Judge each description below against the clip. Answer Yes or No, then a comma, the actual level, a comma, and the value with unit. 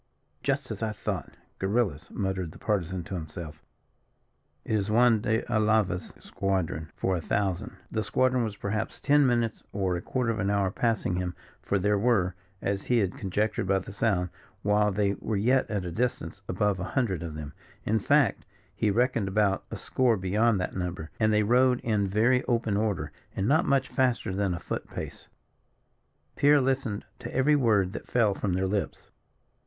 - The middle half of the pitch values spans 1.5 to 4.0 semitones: Yes, average, 3.6 semitones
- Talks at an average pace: Yes, average, 180 wpm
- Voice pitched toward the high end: No, low, 105 Hz